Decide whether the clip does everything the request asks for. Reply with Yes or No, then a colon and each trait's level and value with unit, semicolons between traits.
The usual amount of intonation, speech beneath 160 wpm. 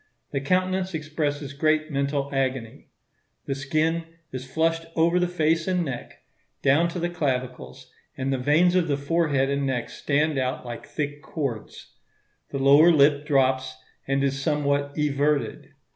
Yes: average, 3.0 semitones; average, 150 wpm